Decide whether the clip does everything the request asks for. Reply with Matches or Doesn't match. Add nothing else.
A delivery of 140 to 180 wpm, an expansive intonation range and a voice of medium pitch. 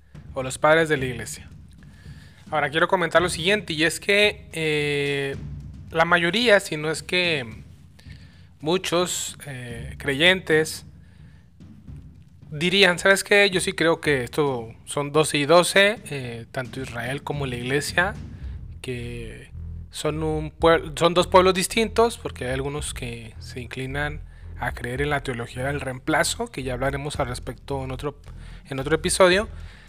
Matches